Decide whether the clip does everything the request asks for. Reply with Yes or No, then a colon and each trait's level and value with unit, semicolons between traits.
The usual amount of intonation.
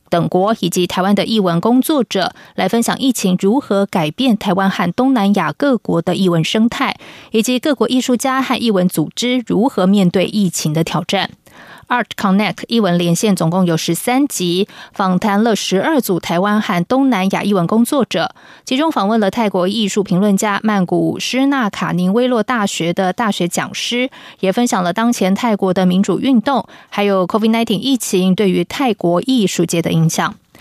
Yes: average, 4.6 semitones